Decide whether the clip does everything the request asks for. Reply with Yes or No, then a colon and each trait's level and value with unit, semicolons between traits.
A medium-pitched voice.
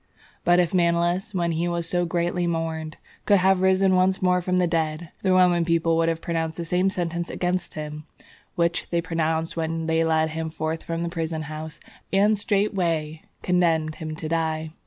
Yes: medium, 170 Hz